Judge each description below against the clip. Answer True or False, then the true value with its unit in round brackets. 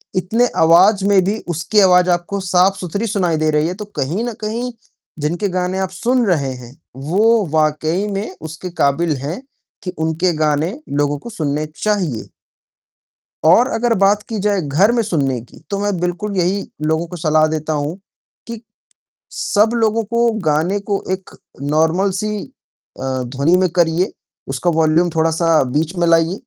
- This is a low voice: False (180 Hz)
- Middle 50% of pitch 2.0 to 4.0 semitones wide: False (4.4 semitones)